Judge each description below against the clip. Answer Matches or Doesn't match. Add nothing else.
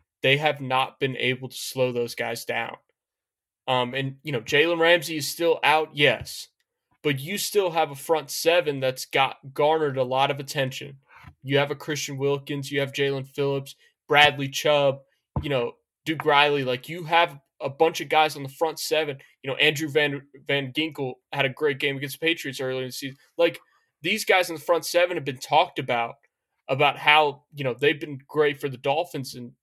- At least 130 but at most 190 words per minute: Doesn't match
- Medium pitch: Matches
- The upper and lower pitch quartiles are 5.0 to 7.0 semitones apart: Doesn't match